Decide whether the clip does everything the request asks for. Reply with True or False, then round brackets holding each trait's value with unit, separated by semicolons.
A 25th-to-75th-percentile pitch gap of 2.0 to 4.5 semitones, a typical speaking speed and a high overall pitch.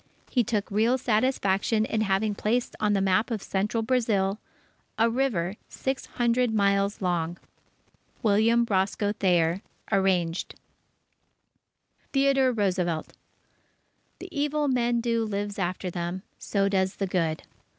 False (3.7 semitones; 120 wpm; 205 Hz)